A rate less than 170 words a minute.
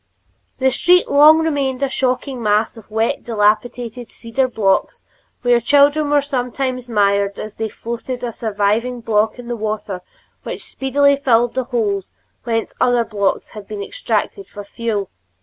Yes: average, 150 wpm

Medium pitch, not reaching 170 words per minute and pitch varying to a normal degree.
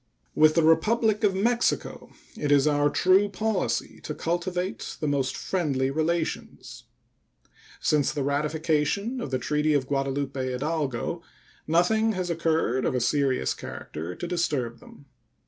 Yes: medium, 155 Hz; slow, 135 wpm; average, 4.5 semitones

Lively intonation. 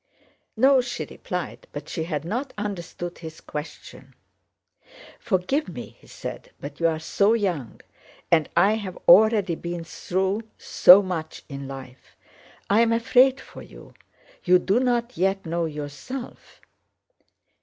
Yes: wide, 5.8 semitones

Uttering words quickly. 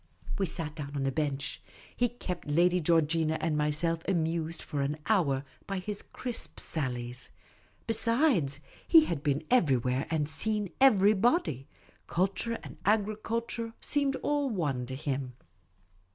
No: slow, 135 wpm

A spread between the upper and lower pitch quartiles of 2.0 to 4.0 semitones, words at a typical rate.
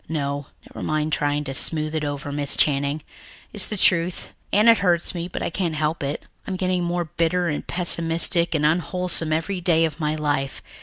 Yes: average, 2.9 semitones; average, 195 wpm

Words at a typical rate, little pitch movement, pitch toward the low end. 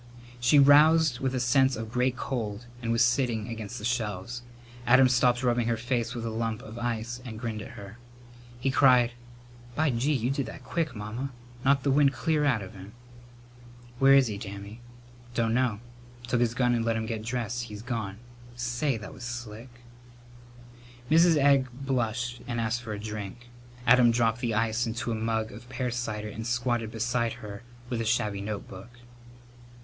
Yes: average, 180 wpm; narrow, 2.3 semitones; low, 120 Hz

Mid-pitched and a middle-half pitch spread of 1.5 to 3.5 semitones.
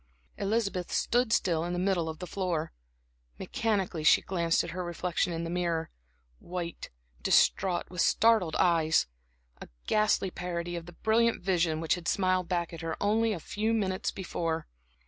Yes: medium, 180 Hz; average, 2.8 semitones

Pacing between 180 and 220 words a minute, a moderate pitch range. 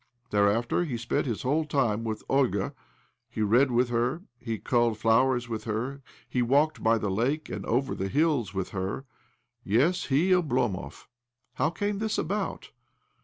No: average, 165 wpm; average, 4.5 semitones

